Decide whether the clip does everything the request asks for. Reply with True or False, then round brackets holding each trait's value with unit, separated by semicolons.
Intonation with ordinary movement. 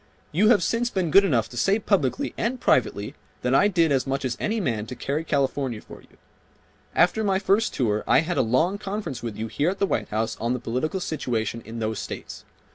False (8.8 semitones)